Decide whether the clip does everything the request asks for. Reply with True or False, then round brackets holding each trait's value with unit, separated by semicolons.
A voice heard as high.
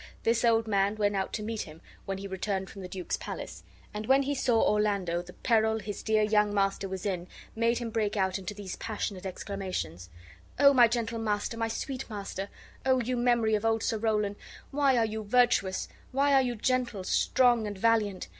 True (215 Hz)